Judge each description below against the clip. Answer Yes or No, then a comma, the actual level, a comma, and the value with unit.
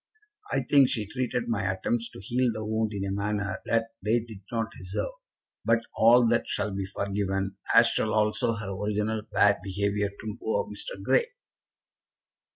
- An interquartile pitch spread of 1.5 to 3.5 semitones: Yes, narrow, 2.4 semitones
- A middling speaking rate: Yes, average, 165 wpm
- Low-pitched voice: Yes, low, 105 Hz